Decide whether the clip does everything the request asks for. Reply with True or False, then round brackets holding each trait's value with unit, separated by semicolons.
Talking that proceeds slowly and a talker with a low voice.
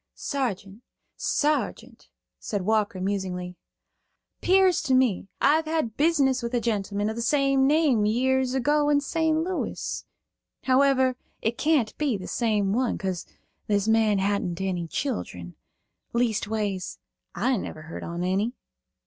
False (130 wpm; 230 Hz)